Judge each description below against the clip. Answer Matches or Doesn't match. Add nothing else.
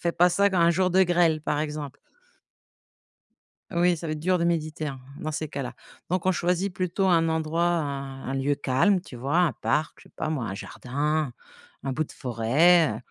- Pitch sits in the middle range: Matches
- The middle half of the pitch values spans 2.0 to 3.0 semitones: Doesn't match